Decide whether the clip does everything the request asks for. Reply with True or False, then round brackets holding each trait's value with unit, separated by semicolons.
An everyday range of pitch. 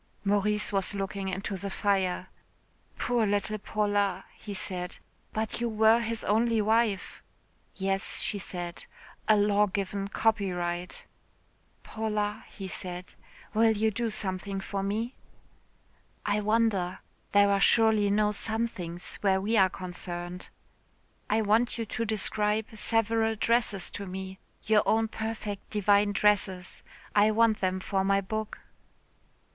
False (2.2 semitones)